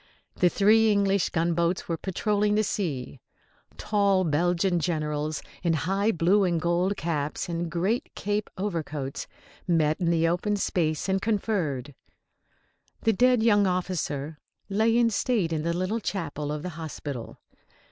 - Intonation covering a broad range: No, average, 4.1 semitones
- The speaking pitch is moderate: Yes, medium, 175 Hz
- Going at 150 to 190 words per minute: No, average, 140 wpm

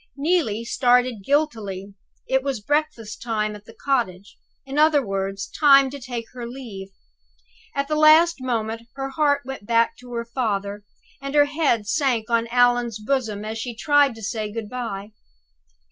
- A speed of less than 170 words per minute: Yes, average, 160 wpm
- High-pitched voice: Yes, high, 240 Hz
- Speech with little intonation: No, average, 4.3 semitones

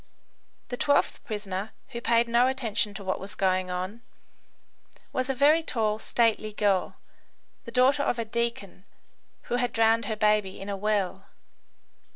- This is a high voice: Yes, high, 220 Hz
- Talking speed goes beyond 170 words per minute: No, average, 155 wpm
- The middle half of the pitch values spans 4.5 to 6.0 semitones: No, average, 3.1 semitones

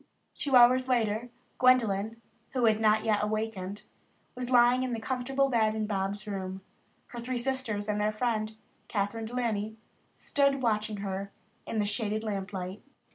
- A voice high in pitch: Yes, high, 220 Hz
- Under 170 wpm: Yes, average, 155 wpm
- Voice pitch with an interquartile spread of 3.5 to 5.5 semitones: No, average, 3.0 semitones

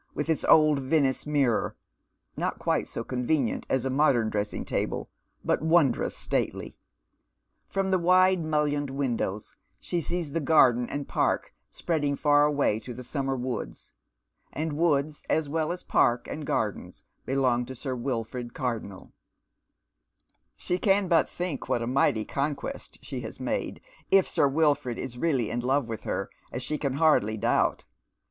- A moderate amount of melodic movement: Yes, average, 4.2 semitones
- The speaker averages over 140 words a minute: Yes, average, 155 wpm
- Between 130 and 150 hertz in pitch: Yes, medium, 140 Hz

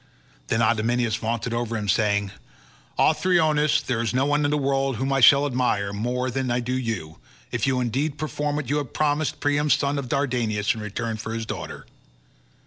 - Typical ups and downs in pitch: Yes, average, 4.1 semitones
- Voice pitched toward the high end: No, low, 125 Hz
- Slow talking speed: No, average, 190 wpm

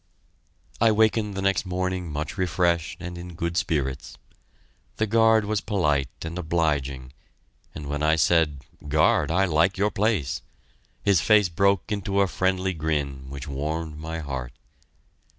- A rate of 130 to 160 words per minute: Yes, average, 145 wpm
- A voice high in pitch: No, very low, 85 Hz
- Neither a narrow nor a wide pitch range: Yes, average, 4.4 semitones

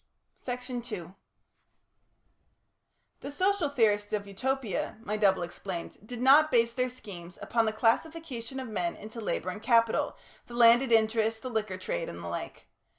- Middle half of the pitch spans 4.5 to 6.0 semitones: No, average, 3.5 semitones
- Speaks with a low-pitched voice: No, high, 230 Hz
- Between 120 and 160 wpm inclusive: Yes, average, 150 wpm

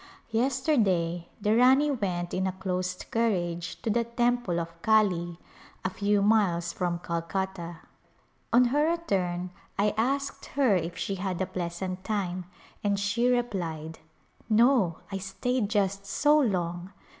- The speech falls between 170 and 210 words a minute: No, average, 140 wpm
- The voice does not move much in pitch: No, average, 5.0 semitones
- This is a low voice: No, high, 195 Hz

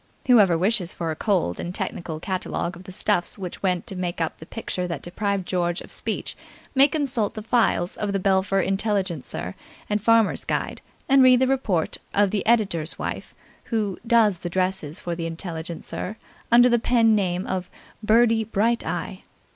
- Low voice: No, high, 195 Hz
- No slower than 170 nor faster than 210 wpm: Yes, average, 175 wpm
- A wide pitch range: No, average, 4.3 semitones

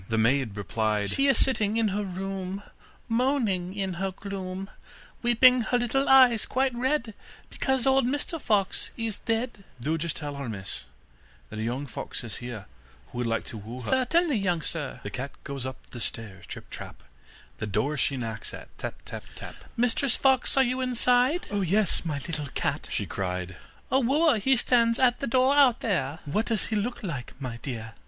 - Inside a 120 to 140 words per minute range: No, average, 190 wpm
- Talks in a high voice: Yes, high, 195 Hz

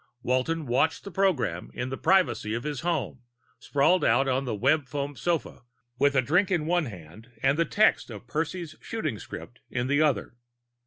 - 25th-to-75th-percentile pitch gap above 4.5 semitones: Yes, average, 5.1 semitones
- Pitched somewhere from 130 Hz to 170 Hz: Yes, medium, 140 Hz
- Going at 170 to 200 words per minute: Yes, average, 175 wpm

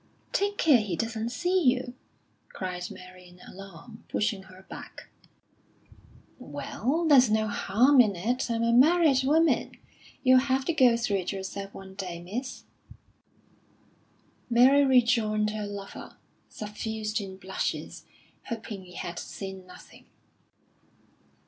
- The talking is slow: Yes, slow, 125 wpm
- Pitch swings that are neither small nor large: Yes, average, 5.0 semitones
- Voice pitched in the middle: No, high, 220 Hz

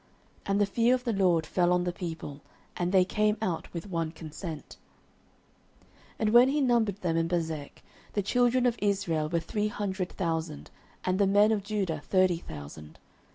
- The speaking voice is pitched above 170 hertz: Yes, medium, 185 Hz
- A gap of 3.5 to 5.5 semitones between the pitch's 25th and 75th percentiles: Yes, average, 4.2 semitones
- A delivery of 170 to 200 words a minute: Yes, average, 180 wpm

